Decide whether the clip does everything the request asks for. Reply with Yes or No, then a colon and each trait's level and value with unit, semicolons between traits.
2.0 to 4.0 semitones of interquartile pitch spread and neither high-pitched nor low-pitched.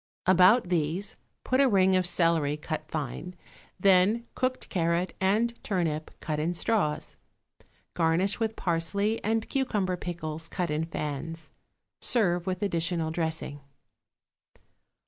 Yes: average, 3.6 semitones; medium, 175 Hz